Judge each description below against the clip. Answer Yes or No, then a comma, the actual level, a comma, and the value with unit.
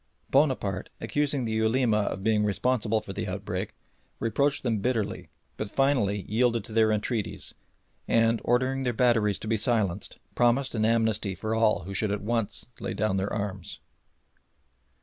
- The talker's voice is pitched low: Yes, low, 110 Hz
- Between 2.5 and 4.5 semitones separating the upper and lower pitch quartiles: Yes, average, 2.8 semitones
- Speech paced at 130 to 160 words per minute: Yes, average, 155 wpm